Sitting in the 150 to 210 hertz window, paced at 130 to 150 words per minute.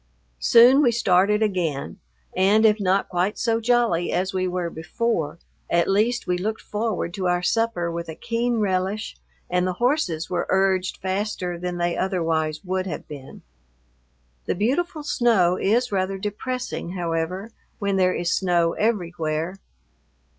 Yes: high, 190 Hz; average, 145 wpm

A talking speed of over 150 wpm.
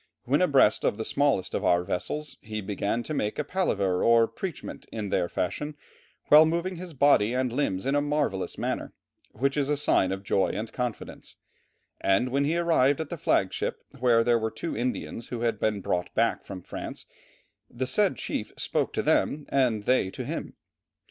Yes: average, 190 wpm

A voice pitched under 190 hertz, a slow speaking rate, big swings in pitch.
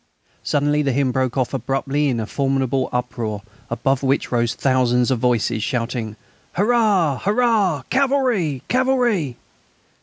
Yes: low, 135 Hz; slow, 125 wpm; wide, 6.9 semitones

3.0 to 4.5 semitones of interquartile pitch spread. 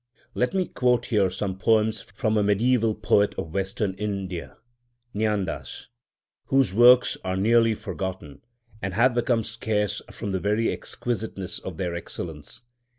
Yes: average, 3.9 semitones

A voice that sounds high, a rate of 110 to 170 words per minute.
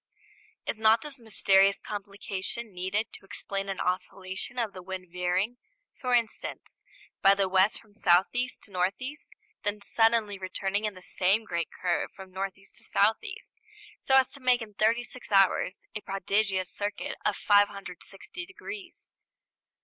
Yes: high, 200 Hz; average, 160 wpm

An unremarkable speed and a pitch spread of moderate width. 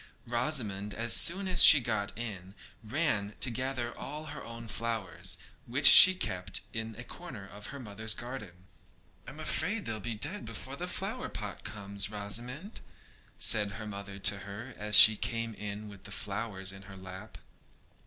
Yes: average, 170 wpm; average, 3.1 semitones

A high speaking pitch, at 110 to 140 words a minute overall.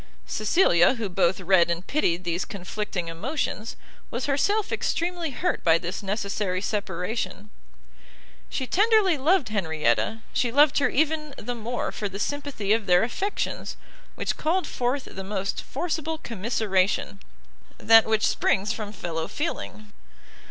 Yes: high, 215 Hz; slow, 135 wpm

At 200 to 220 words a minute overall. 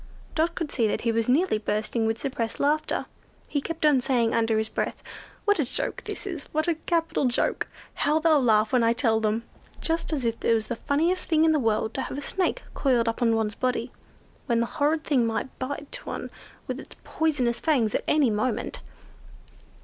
Yes: fast, 205 wpm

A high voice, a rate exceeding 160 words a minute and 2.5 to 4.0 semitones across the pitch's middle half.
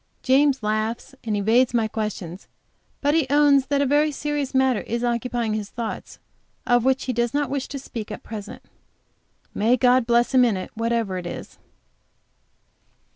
Yes: high, 240 Hz; average, 170 wpm; average, 3.5 semitones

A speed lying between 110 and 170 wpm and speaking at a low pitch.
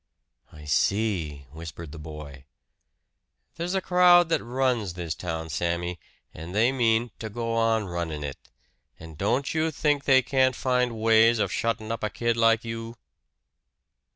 Yes: average, 155 wpm; low, 115 Hz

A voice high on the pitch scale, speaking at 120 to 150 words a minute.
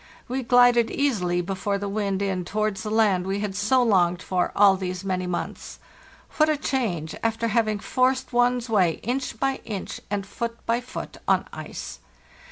No: high, 210 Hz; average, 175 wpm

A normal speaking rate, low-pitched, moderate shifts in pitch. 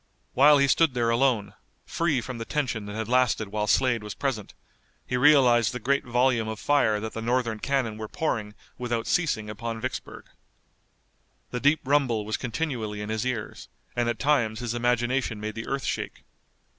Yes: average, 180 wpm; low, 120 Hz; average, 3.3 semitones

